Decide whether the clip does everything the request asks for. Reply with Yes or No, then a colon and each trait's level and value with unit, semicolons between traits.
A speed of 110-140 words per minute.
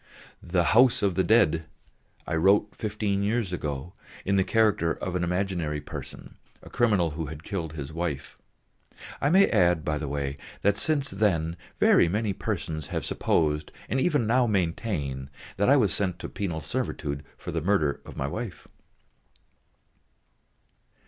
No: average, 155 wpm